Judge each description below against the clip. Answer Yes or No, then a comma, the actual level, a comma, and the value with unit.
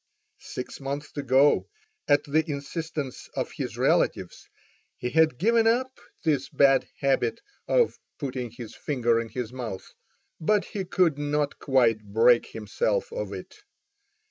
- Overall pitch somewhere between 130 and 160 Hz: Yes, medium, 140 Hz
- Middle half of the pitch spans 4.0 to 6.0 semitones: Yes, average, 4.7 semitones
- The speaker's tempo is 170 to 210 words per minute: No, slow, 135 wpm